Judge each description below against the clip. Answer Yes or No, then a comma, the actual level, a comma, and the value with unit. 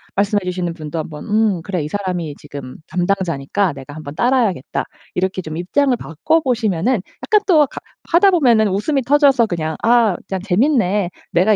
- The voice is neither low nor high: No, high, 195 Hz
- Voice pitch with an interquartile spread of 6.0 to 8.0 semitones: Yes, wide, 6.4 semitones